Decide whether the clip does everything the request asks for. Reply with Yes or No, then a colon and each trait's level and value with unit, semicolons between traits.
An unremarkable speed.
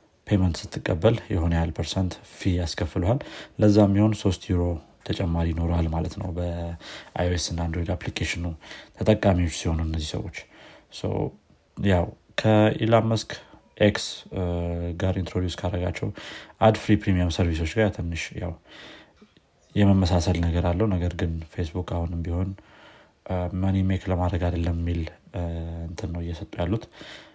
No: fast, 120 wpm